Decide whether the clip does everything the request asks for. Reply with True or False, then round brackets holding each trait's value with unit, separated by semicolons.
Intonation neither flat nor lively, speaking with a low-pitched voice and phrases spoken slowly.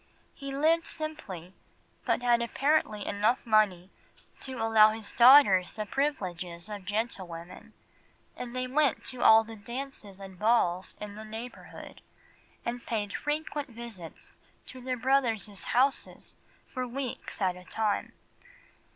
False (4.2 semitones; 225 Hz; 130 wpm)